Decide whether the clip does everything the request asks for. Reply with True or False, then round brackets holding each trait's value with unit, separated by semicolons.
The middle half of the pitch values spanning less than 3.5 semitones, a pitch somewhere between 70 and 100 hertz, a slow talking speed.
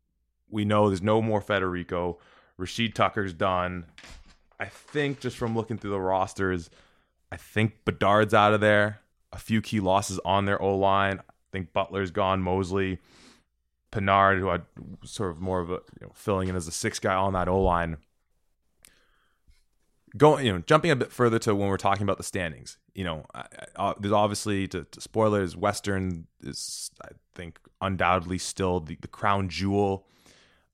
False (2.6 semitones; 95 Hz; 175 wpm)